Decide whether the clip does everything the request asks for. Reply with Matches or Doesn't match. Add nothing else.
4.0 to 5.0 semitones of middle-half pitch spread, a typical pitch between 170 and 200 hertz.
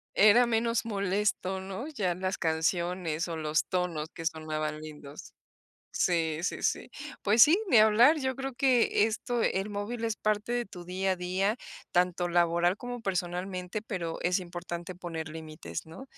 Matches